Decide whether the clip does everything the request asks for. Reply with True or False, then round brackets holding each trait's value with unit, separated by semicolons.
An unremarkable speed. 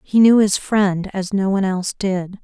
False (220 wpm)